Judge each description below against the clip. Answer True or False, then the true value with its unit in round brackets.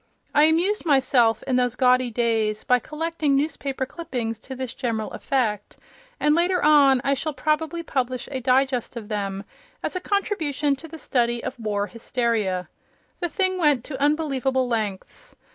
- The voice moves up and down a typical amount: True (4.5 semitones)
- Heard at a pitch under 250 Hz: False (260 Hz)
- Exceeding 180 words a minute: False (160 wpm)